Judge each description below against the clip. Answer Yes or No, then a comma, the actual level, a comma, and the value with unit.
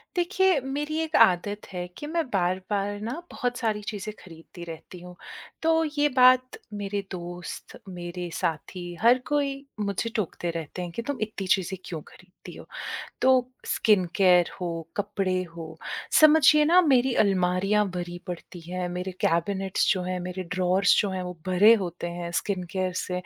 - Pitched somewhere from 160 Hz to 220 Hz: Yes, high, 190 Hz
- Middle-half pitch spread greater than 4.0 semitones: Yes, average, 4.6 semitones